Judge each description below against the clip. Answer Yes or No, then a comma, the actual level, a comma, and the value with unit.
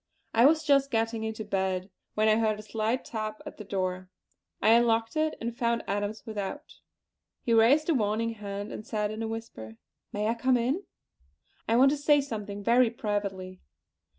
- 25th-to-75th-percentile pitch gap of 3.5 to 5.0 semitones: No, narrow, 2.4 semitones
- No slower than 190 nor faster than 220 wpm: No, average, 180 wpm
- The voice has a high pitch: Yes, high, 225 Hz